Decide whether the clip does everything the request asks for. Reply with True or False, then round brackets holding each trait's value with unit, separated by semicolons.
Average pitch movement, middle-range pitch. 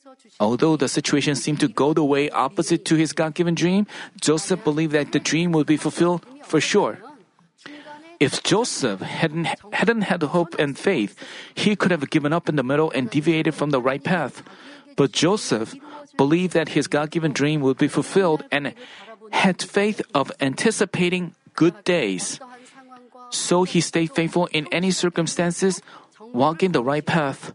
True (4.6 semitones; 170 Hz)